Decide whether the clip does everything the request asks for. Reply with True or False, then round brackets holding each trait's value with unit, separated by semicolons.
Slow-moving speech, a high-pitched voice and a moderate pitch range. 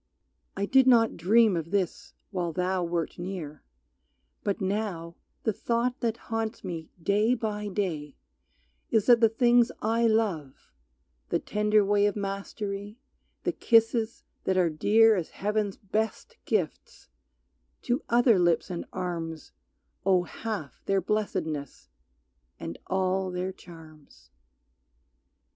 True (125 wpm; 200 Hz; 4.1 semitones)